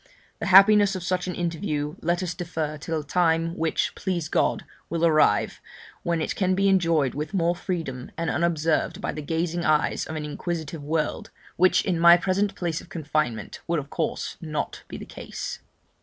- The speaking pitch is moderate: Yes, medium, 165 Hz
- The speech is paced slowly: No, average, 185 wpm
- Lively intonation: No, narrow, 2.6 semitones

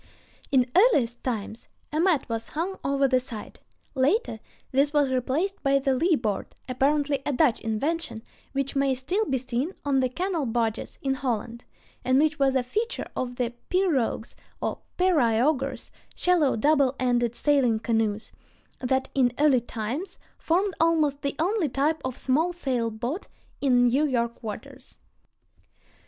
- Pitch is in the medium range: No, very high, 270 Hz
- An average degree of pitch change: Yes, average, 4.1 semitones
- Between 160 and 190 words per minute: No, average, 145 wpm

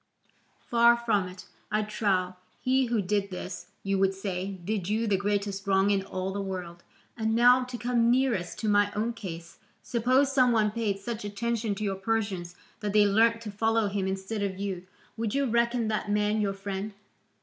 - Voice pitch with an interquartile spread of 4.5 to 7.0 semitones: No, average, 2.9 semitones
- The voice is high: Yes, high, 210 Hz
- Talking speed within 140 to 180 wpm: No, average, 190 wpm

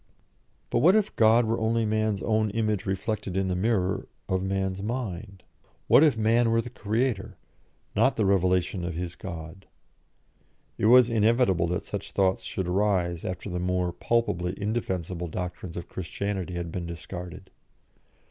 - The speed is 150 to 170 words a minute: Yes, average, 155 wpm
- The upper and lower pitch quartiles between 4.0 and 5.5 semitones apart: No, average, 3.6 semitones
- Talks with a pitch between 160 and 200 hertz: No, very low, 95 Hz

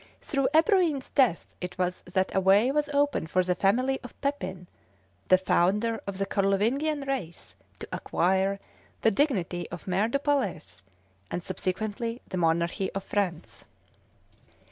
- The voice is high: Yes, high, 200 Hz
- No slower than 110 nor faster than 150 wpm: Yes, average, 145 wpm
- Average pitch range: No, wide, 6.6 semitones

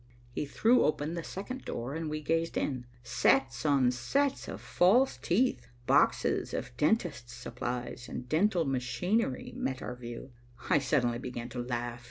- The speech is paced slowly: No, average, 155 wpm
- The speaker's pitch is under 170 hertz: Yes, low, 135 Hz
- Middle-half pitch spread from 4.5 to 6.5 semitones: Yes, wide, 5.6 semitones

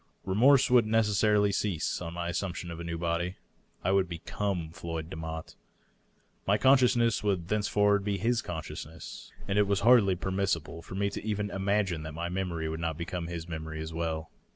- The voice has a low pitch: Yes, very low, 95 Hz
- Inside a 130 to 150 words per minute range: No, average, 185 wpm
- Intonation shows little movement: No, average, 3.8 semitones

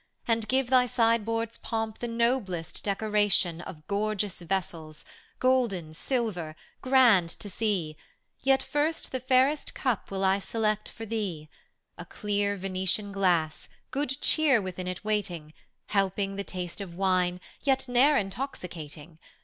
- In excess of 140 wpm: No, slow, 135 wpm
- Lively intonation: No, average, 4.8 semitones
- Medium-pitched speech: No, high, 205 Hz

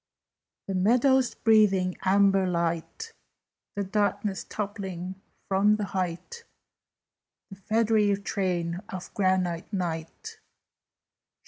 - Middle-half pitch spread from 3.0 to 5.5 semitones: No, narrow, 2.4 semitones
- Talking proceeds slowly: Yes, slow, 90 wpm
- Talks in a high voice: Yes, high, 195 Hz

